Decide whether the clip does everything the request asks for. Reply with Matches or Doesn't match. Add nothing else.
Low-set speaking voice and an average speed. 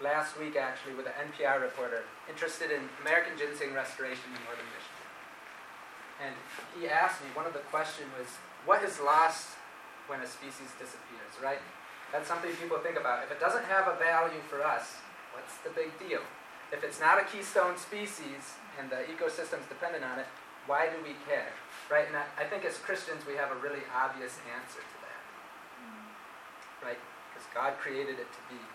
Doesn't match